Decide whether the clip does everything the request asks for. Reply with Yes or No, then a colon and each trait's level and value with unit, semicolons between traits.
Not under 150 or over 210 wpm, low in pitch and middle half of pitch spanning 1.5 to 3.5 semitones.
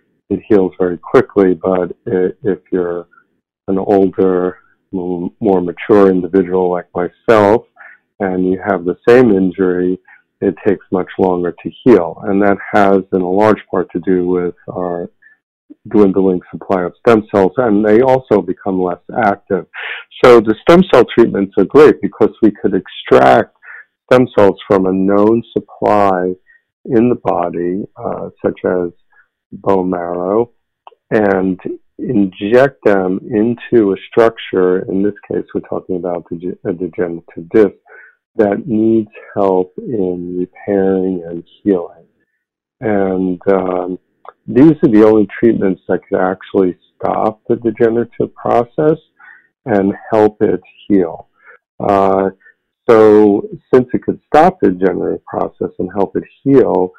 No: slow, 135 wpm; very low, 95 Hz; narrow, 2.6 semitones